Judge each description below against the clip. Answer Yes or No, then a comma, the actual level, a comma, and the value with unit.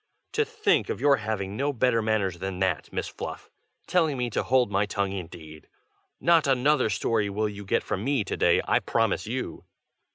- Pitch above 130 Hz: No, low, 110 Hz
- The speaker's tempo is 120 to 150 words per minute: No, average, 190 wpm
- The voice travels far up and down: Yes, wide, 5.7 semitones